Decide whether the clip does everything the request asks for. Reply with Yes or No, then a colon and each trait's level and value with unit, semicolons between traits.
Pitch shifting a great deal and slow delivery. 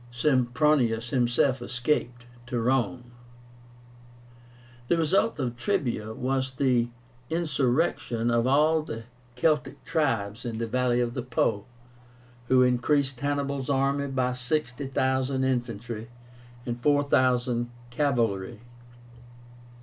No: average, 2.7 semitones; slow, 100 wpm